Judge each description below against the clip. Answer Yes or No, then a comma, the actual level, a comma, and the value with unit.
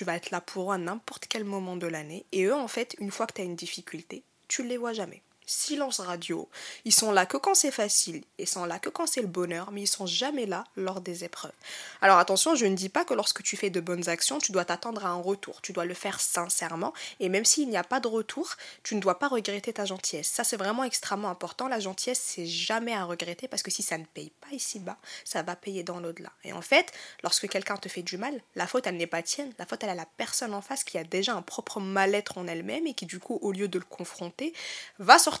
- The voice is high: Yes, high, 200 Hz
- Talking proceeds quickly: Yes, fast, 270 wpm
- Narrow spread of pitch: No, average, 5.0 semitones